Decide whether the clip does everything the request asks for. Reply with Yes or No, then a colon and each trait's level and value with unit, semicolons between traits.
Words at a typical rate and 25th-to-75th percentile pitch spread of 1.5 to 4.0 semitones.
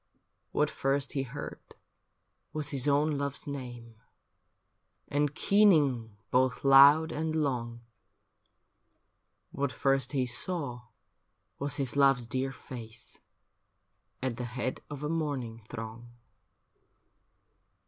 No: slow, 105 wpm; average, 2.9 semitones